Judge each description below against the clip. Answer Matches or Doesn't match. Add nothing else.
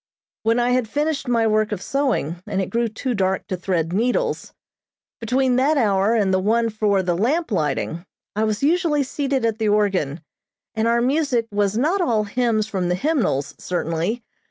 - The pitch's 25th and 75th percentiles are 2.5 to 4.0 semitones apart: Doesn't match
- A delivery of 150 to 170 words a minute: Doesn't match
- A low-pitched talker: Doesn't match